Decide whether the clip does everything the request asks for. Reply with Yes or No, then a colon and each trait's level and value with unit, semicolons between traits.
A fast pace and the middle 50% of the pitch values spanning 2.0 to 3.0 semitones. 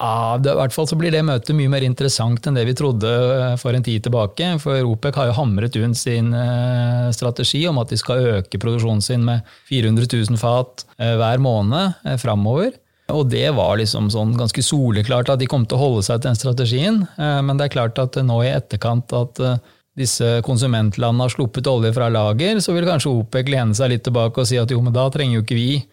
Yes: fast, 210 wpm; narrow, 2.4 semitones